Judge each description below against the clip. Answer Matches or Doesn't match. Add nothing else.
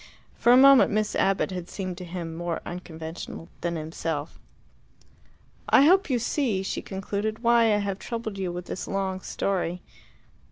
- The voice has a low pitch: Doesn't match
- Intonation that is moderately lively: Matches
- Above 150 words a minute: Matches